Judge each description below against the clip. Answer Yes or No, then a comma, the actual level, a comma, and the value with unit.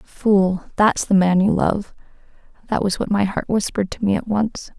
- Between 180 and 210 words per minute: Yes, average, 200 wpm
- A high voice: Yes, high, 200 Hz